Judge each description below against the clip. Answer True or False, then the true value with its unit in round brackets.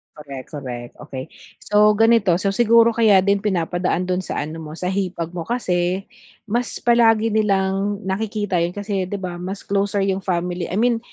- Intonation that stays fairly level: False (3.1 semitones)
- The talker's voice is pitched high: True (195 Hz)